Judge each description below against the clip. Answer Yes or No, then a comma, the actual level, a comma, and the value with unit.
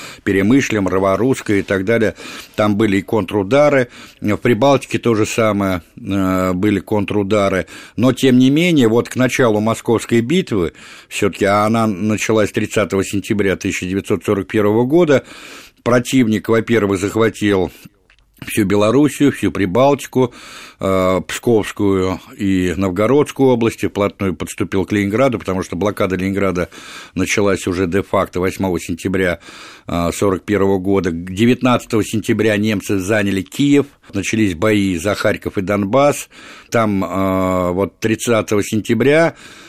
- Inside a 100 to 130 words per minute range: Yes, average, 115 wpm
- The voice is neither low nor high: No, low, 105 Hz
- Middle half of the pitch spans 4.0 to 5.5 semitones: No, average, 3.2 semitones